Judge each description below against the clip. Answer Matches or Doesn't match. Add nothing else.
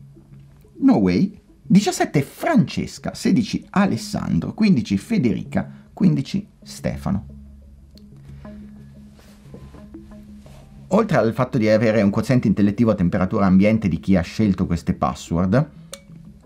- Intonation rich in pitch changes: Matches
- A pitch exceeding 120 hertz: Doesn't match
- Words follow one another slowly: Matches